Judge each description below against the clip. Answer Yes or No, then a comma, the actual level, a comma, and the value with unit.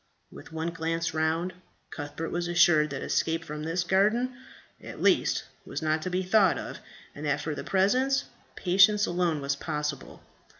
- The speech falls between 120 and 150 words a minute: No, average, 165 wpm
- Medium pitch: Yes, medium, 165 Hz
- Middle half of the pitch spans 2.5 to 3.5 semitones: Yes, average, 3.2 semitones